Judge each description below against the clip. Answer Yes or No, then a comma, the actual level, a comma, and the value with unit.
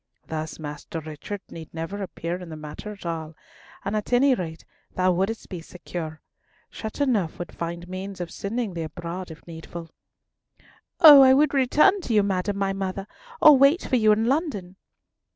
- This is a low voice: No, medium, 185 Hz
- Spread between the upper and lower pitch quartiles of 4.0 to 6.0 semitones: Yes, average, 5.2 semitones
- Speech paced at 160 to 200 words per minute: Yes, average, 170 wpm